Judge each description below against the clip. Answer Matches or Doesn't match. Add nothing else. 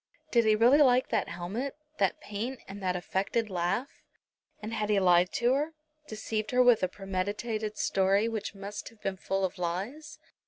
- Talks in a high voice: Matches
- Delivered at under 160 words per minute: Doesn't match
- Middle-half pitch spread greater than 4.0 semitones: Doesn't match